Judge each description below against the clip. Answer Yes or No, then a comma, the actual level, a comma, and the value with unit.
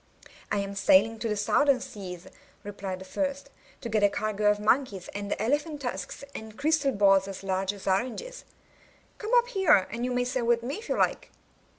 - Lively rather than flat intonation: Yes, wide, 5.7 semitones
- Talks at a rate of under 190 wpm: No, average, 195 wpm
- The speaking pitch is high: Yes, high, 220 Hz